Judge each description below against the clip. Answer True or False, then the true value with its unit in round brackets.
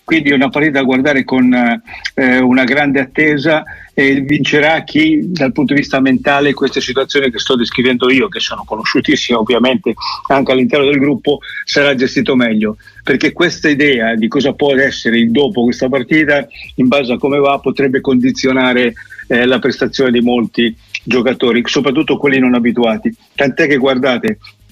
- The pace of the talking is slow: False (165 wpm)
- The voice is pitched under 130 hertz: False (135 Hz)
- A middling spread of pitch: False (2.3 semitones)